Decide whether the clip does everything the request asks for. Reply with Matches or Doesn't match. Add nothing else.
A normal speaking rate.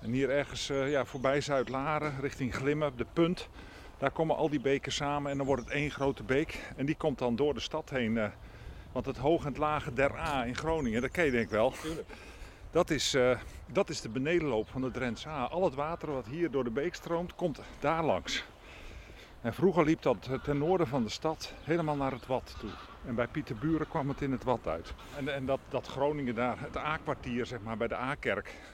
Doesn't match